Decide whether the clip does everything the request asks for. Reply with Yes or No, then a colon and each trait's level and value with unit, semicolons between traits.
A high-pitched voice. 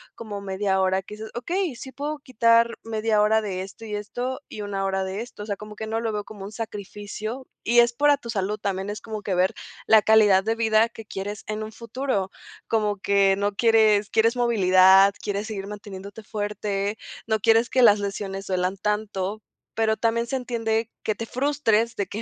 Yes: high, 215 Hz